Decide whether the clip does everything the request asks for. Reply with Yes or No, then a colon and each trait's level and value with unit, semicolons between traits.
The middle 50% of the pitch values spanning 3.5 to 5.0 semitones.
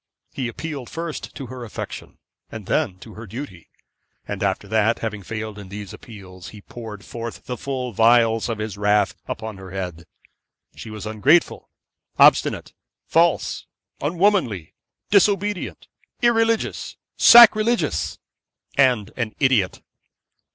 No: wide, 5.5 semitones